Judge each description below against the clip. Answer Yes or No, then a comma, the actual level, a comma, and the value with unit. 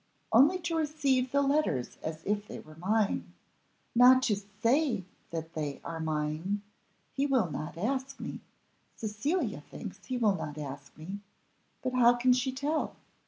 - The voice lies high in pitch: Yes, high, 220 Hz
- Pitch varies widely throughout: Yes, wide, 8.2 semitones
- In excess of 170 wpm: No, average, 155 wpm